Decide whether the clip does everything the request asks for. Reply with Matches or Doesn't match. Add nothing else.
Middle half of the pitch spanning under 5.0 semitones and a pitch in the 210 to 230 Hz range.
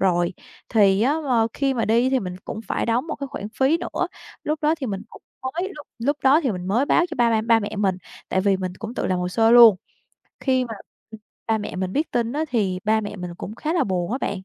Doesn't match